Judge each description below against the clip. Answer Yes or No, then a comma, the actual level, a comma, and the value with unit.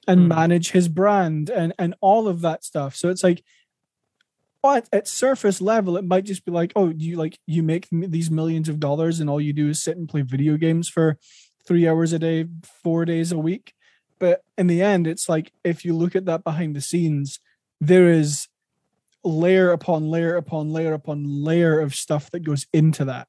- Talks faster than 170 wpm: Yes, fast, 205 wpm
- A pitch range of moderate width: No, narrow, 2.3 semitones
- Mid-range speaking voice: Yes, medium, 165 Hz